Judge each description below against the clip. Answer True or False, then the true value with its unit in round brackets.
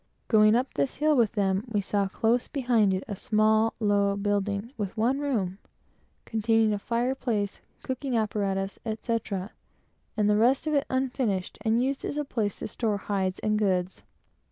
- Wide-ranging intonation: False (3.2 semitones)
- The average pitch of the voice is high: True (215 Hz)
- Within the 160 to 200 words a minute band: True (170 wpm)